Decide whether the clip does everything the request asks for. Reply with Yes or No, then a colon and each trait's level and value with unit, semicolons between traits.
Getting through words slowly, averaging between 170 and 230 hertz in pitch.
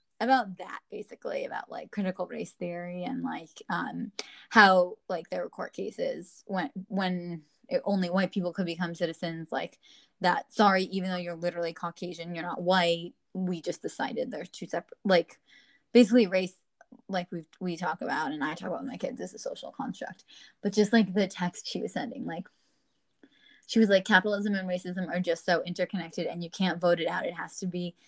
No: average, 195 wpm; medium, 185 Hz